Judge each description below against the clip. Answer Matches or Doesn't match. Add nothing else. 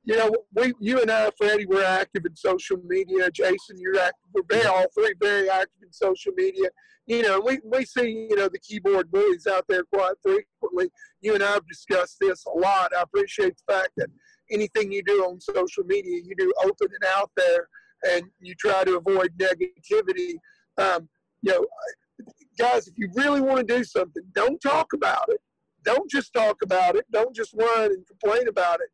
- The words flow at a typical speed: Matches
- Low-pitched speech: Doesn't match